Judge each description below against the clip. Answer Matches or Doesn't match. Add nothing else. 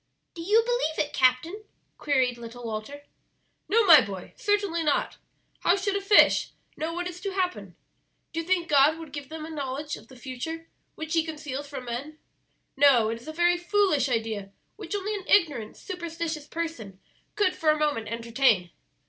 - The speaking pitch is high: Matches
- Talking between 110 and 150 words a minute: Doesn't match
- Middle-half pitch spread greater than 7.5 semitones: Doesn't match